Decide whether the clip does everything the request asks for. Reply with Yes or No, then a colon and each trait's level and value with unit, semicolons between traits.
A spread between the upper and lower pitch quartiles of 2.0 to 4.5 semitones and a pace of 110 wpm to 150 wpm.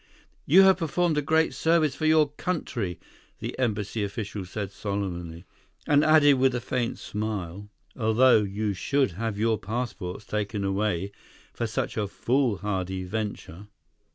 No: average, 5.3 semitones; average, 140 wpm